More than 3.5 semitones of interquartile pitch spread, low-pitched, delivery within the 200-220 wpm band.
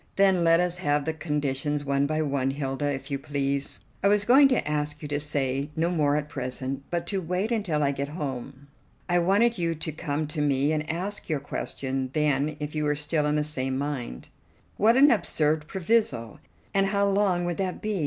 No: average, 4.2 semitones; medium, 150 Hz; fast, 205 wpm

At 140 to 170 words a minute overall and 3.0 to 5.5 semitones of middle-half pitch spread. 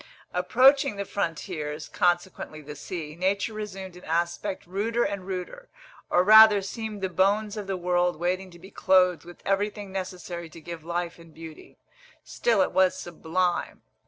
No: average, 160 wpm; narrow, 2.6 semitones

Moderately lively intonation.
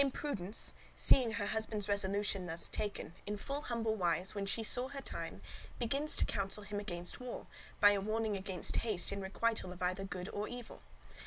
Yes: average, 3.2 semitones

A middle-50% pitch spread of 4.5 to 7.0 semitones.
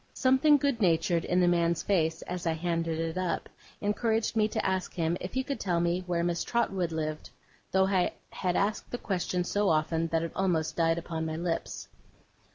No: average, 2.9 semitones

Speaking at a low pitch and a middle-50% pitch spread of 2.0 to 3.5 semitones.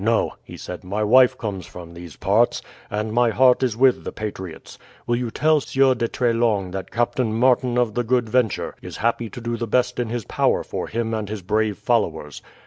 Yes: low, 115 Hz; average, 2.9 semitones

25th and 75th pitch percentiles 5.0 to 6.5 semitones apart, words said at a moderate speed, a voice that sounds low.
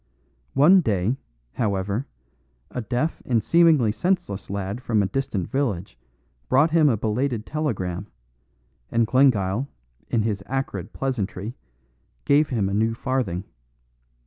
No: average, 5.3 semitones; slow, 120 wpm; low, 115 Hz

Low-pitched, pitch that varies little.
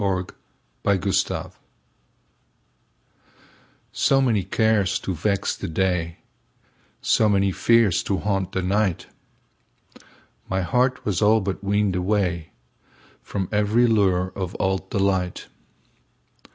Yes: very low, 95 Hz; narrow, 2.1 semitones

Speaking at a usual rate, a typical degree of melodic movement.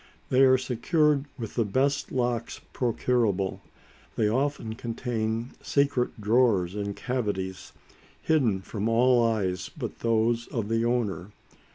No: slow, 125 wpm; average, 3.3 semitones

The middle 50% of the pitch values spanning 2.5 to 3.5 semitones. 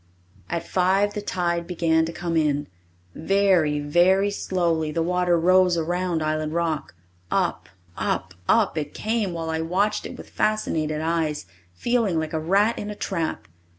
Yes: average, 3.1 semitones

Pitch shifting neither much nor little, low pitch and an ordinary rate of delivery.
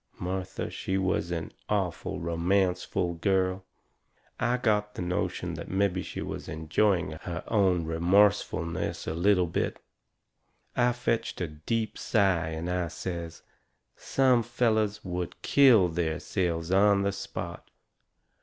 No: average, 3.4 semitones; very low, 95 Hz; slow, 125 wpm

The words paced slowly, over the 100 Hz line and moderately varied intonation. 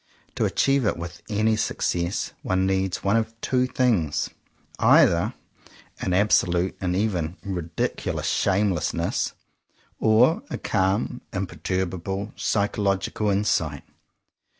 No: slow, 105 wpm; very low, 95 Hz; average, 3.2 semitones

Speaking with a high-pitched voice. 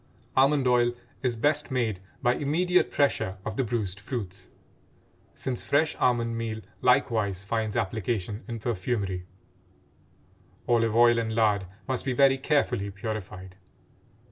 No: low, 115 Hz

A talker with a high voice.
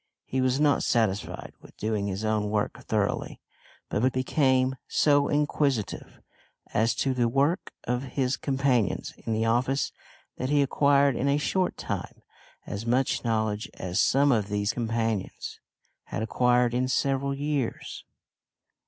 No: low, 125 Hz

